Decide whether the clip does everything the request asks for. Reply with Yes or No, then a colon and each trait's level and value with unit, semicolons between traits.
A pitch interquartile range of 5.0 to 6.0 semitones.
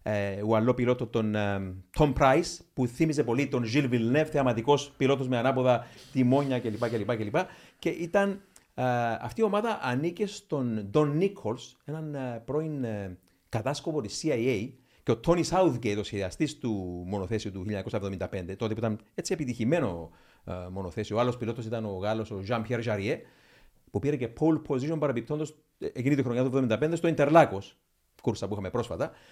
Yes: wide, 5.6 semitones